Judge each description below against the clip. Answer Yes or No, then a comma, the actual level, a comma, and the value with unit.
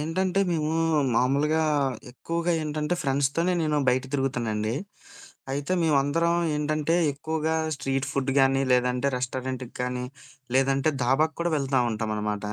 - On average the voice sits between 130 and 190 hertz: Yes, medium, 140 Hz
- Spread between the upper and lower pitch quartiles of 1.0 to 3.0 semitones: No, average, 3.5 semitones